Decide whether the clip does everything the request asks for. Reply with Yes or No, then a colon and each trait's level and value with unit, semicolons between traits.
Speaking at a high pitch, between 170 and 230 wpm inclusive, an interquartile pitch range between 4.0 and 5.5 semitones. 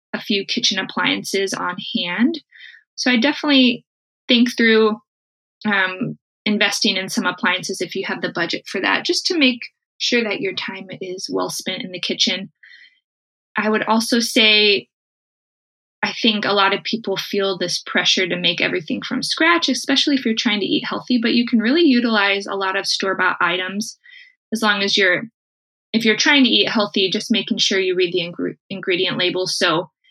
Yes: high, 215 Hz; average, 180 wpm; average, 4.6 semitones